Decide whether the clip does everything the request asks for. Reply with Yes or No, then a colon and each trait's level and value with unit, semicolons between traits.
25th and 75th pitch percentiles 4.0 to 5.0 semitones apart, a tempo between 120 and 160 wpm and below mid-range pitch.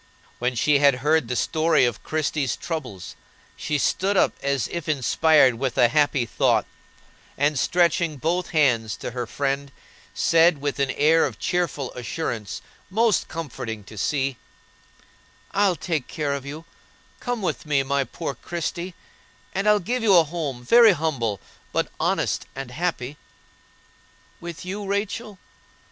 No: average, 4.6 semitones; average, 145 wpm; medium, 150 Hz